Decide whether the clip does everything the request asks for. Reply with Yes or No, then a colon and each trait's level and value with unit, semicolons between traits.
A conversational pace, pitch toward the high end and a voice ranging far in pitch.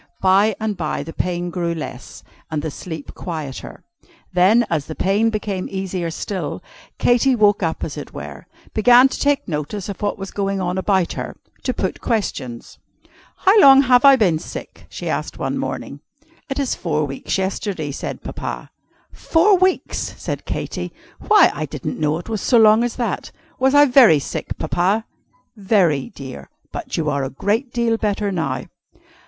Yes: average, 170 wpm; high, 195 Hz; wide, 6.1 semitones